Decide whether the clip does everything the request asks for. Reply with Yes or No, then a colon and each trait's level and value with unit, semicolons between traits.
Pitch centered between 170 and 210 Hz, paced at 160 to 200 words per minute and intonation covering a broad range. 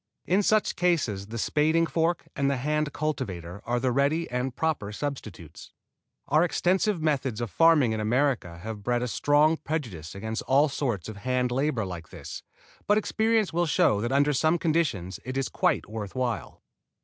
No: low, 135 Hz; average, 175 wpm; wide, 6.1 semitones